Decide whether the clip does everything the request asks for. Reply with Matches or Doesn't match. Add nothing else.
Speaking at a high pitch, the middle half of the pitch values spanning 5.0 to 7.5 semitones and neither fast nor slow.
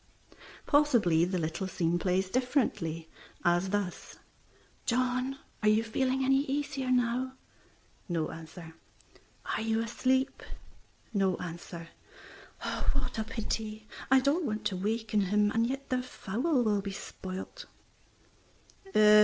Doesn't match